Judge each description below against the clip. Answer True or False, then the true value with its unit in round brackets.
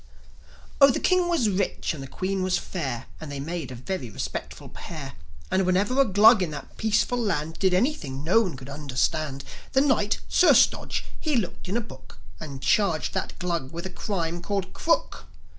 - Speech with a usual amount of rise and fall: False (6.2 semitones)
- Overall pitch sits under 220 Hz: True (185 Hz)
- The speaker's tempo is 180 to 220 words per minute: True (190 wpm)